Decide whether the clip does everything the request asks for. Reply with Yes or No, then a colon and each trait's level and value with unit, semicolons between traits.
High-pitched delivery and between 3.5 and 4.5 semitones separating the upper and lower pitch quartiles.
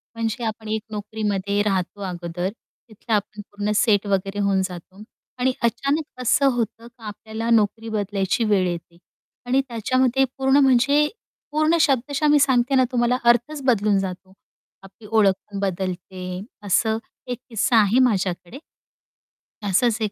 Yes: high, 220 Hz; average, 3.9 semitones